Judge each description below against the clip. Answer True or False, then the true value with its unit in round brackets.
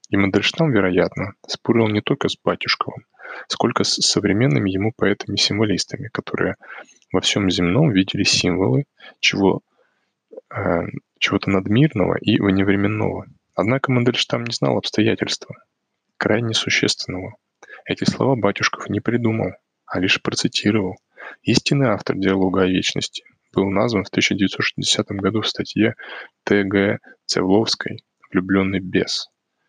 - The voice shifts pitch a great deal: False (3.5 semitones)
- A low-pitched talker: True (100 Hz)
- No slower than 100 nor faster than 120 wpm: True (115 wpm)